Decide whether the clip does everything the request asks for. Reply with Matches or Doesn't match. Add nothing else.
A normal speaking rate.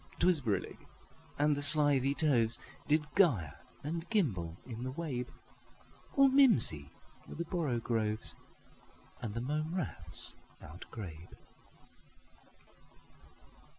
Doesn't match